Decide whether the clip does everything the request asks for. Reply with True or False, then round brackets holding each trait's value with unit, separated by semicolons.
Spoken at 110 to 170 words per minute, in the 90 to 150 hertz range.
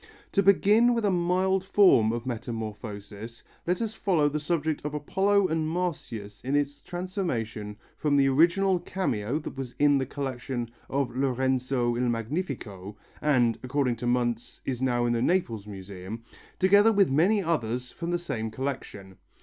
True (160 wpm; 135 Hz)